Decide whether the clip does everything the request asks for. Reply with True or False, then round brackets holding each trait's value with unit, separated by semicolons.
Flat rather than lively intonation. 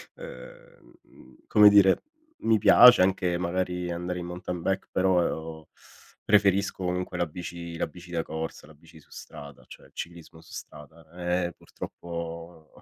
True (1.8 semitones)